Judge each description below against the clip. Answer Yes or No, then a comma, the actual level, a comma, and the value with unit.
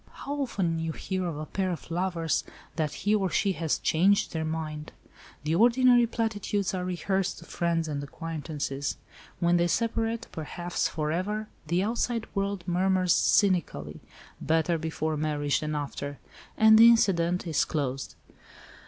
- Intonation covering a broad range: No, average, 4.2 semitones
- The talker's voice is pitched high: No, medium, 175 Hz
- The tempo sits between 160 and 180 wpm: No, average, 145 wpm